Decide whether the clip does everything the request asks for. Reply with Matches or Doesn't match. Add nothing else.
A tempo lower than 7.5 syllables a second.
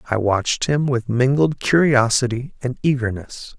Matches